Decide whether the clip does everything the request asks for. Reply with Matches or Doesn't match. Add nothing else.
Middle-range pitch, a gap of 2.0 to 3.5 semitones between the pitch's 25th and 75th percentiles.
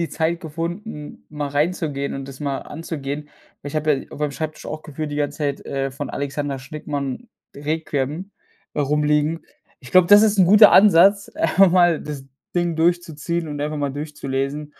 Matches